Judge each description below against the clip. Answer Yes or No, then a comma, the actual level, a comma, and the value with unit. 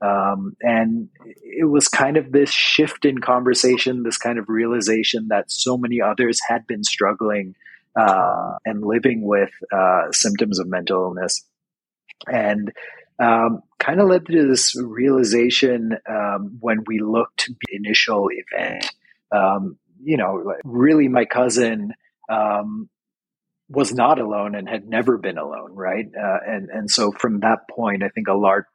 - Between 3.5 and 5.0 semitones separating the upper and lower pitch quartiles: Yes, average, 3.9 semitones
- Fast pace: No, average, 150 wpm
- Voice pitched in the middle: No, low, 120 Hz